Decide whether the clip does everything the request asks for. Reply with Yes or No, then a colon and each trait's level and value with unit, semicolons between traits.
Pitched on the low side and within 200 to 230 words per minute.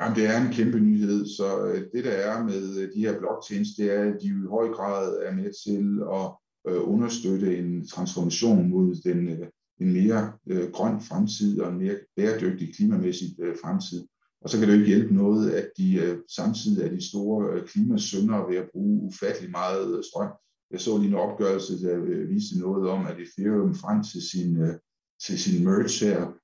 No: low, 110 Hz; average, 180 wpm